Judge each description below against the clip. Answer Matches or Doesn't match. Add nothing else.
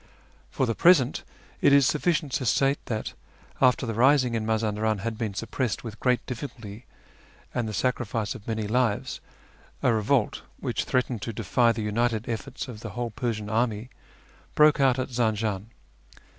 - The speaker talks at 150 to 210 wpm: Matches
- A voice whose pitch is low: Matches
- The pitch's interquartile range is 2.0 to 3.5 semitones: Matches